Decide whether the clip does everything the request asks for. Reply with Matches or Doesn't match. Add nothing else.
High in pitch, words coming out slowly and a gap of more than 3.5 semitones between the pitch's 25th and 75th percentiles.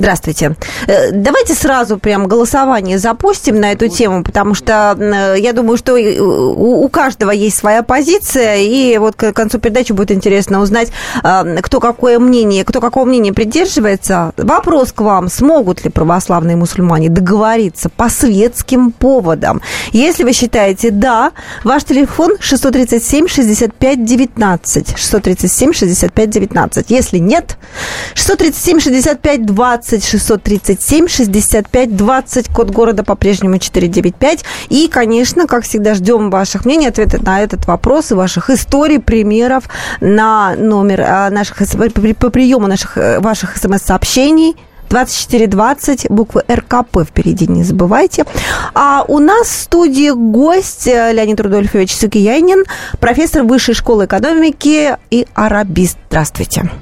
Doesn't match